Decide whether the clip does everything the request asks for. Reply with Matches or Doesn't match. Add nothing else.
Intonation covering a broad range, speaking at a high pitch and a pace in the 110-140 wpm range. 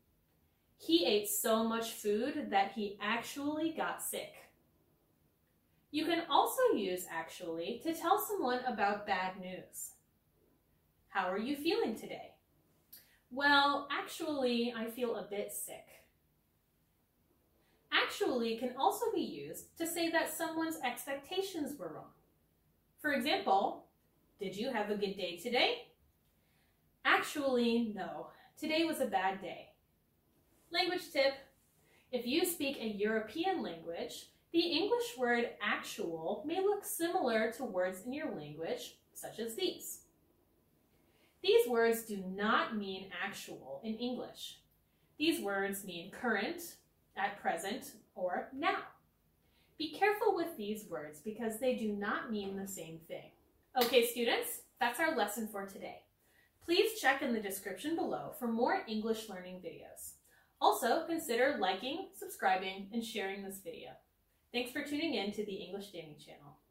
Matches